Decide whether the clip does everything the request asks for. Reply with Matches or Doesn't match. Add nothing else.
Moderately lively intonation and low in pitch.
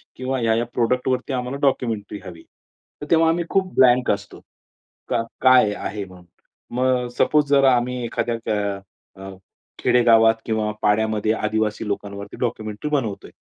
Matches